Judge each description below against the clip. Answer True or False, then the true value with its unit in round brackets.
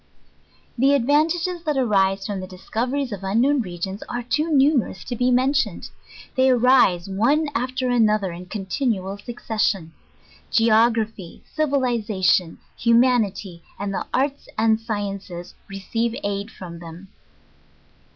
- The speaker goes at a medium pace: False (120 wpm)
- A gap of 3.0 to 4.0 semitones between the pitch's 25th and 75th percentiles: False (5.0 semitones)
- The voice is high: True (225 Hz)